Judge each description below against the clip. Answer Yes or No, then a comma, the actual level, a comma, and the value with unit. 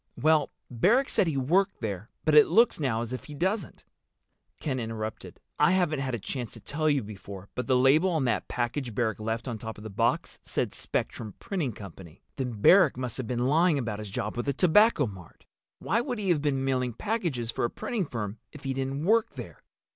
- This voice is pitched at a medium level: No, low, 130 Hz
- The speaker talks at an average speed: No, fast, 215 wpm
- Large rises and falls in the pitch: Yes, wide, 5.9 semitones